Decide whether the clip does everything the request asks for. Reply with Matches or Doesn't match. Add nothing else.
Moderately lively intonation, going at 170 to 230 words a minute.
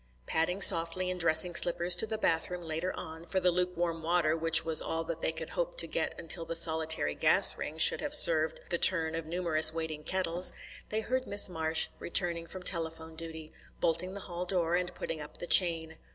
Doesn't match